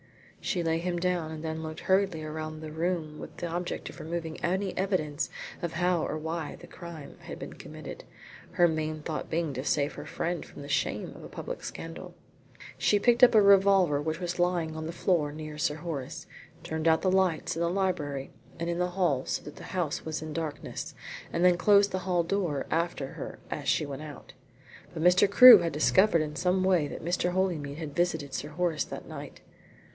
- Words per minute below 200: No, fast, 205 wpm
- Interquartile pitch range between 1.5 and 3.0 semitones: Yes, narrow, 2.6 semitones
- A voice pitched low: No, medium, 165 Hz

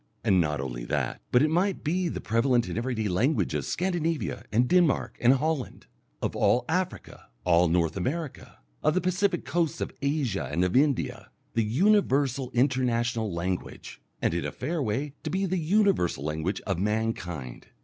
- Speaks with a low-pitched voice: Yes, low, 125 Hz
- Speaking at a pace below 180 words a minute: Yes, average, 170 wpm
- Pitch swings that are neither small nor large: No, wide, 8.5 semitones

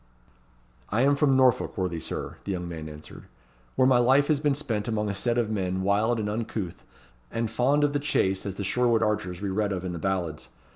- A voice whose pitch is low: Yes, low, 105 Hz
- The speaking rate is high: Yes, fast, 220 wpm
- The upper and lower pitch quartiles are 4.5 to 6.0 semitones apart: Yes, average, 4.8 semitones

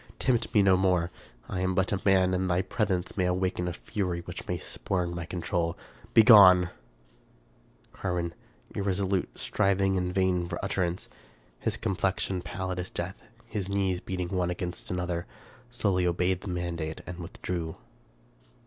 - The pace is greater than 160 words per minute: No, average, 150 wpm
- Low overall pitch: Yes, very low, 90 Hz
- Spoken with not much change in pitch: Yes, narrow, 1.5 semitones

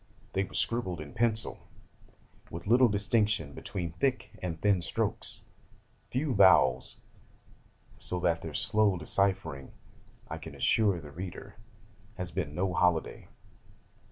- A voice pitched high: No, very low, 95 Hz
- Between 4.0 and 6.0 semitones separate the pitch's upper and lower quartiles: Yes, average, 4.3 semitones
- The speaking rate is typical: No, slow, 125 wpm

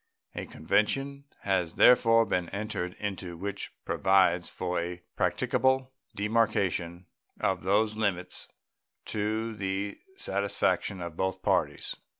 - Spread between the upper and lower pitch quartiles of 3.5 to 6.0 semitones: No, average, 3.1 semitones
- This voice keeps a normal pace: No, slow, 110 wpm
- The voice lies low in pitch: Yes, low, 100 Hz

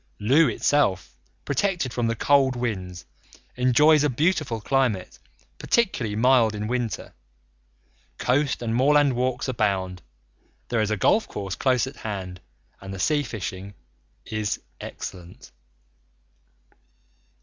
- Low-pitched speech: Yes, low, 120 Hz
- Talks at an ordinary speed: No, slow, 115 wpm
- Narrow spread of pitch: No, average, 4.9 semitones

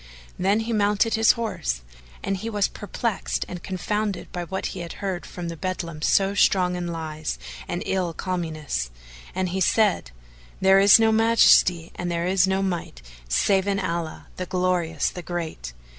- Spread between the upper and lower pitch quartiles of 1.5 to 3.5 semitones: Yes, average, 2.9 semitones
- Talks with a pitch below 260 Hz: Yes, medium, 185 Hz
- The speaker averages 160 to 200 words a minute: Yes, average, 175 wpm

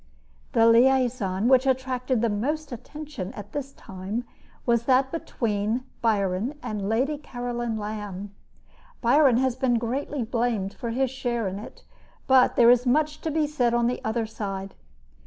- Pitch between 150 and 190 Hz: No, high, 240 Hz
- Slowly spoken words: No, average, 155 wpm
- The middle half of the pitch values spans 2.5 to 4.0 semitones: Yes, average, 3.4 semitones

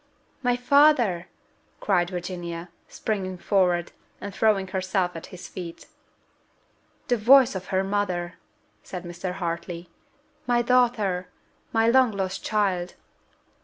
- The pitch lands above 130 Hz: Yes, high, 190 Hz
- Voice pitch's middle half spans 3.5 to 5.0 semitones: Yes, average, 3.9 semitones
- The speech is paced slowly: Yes, slow, 115 wpm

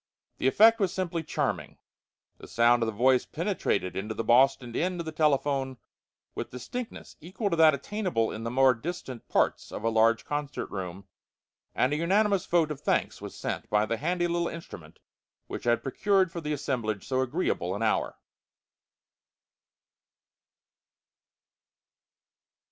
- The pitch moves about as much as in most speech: No, wide, 6.8 semitones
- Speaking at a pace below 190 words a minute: Yes, average, 155 wpm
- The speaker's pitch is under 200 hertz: Yes, low, 135 Hz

